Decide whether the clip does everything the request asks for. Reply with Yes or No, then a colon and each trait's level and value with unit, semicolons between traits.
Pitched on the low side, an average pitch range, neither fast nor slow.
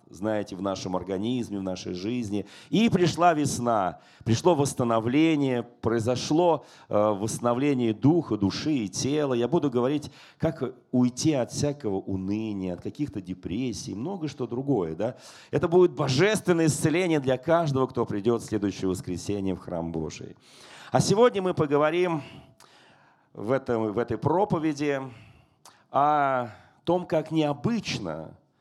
No: low, 130 Hz; wide, 6.3 semitones; average, 125 wpm